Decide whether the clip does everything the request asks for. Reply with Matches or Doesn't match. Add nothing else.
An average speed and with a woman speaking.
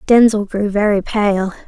Matches